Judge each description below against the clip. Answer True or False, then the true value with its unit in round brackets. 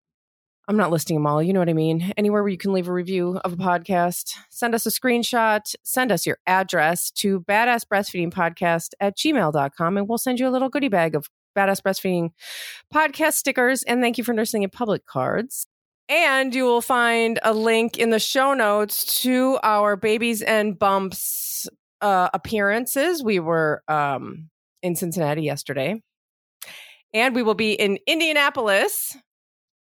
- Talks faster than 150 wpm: True (165 wpm)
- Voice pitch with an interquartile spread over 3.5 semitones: True (5.0 semitones)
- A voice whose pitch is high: True (205 Hz)